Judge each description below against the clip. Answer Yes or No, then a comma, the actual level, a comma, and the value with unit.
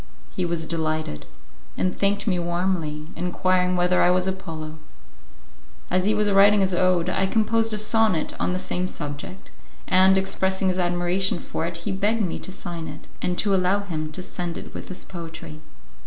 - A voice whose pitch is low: No, medium, 180 Hz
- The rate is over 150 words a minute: Yes, average, 180 wpm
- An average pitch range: No, narrow, 2.2 semitones